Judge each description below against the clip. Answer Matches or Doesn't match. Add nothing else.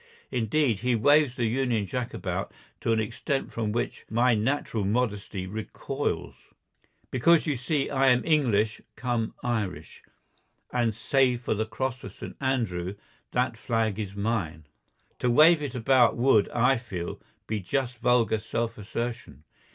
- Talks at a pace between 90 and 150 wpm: Matches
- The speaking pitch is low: Matches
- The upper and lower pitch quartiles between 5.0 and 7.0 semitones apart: Doesn't match